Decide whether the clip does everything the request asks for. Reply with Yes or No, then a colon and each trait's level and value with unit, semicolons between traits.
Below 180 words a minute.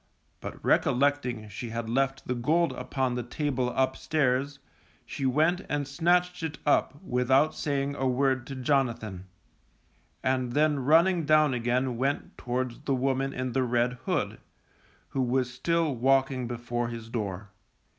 Yes: average, 145 wpm